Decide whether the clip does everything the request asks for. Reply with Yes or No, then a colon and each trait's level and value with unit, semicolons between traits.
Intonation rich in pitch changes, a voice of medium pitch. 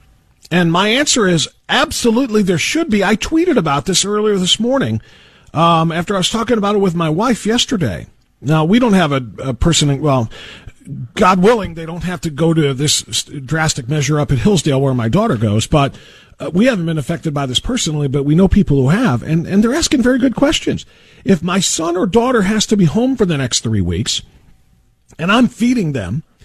Yes: wide, 7.2 semitones; medium, 170 Hz